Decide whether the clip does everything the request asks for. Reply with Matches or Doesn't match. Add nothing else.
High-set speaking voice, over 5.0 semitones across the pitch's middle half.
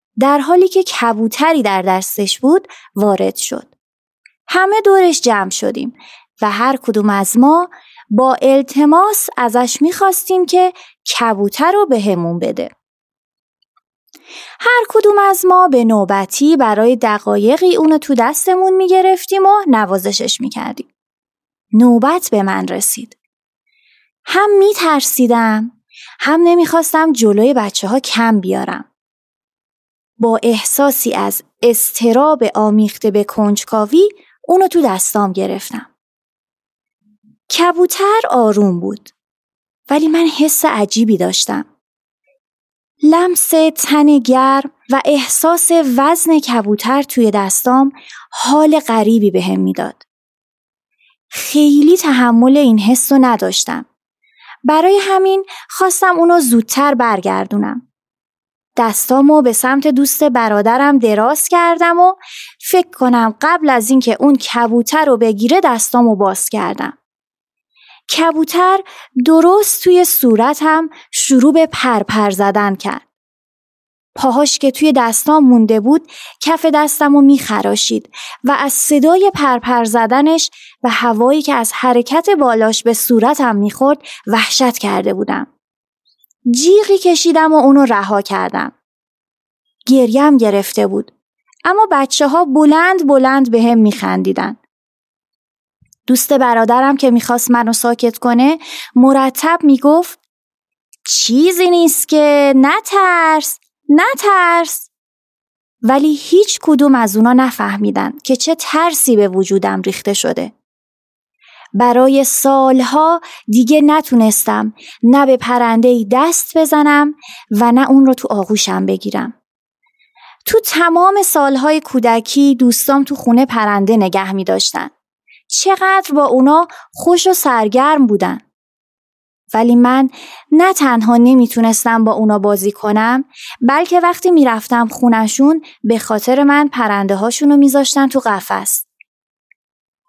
Matches